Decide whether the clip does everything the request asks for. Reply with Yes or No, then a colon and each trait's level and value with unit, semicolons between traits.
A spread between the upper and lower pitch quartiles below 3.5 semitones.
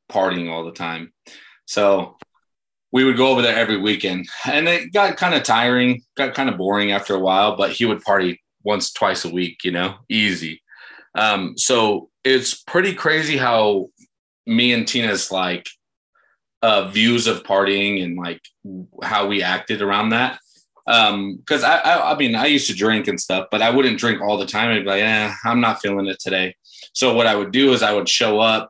No: average, 4.2 semitones